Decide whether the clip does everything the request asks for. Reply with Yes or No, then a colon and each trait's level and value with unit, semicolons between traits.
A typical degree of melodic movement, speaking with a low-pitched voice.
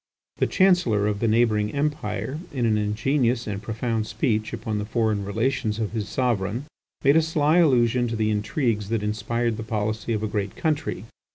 Yes: average, 3.1 semitones; low, 110 Hz